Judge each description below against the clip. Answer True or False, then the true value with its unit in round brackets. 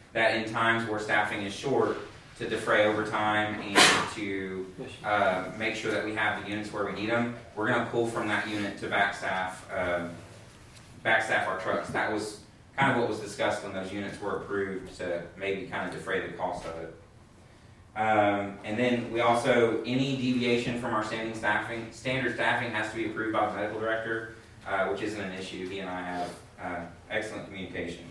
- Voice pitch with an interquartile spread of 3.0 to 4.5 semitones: False (2.6 semitones)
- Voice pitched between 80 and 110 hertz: True (105 Hz)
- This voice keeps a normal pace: True (195 wpm)